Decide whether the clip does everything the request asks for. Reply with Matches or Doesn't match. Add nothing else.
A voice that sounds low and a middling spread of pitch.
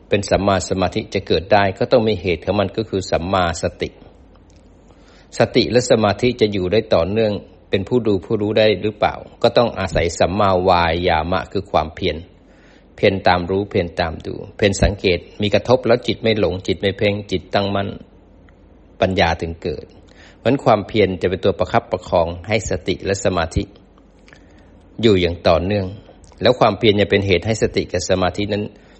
Matches